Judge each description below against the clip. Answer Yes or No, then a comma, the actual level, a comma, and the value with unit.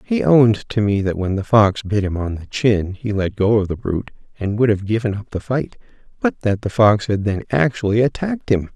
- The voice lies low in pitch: Yes, low, 110 Hz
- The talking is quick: Yes, fast, 240 wpm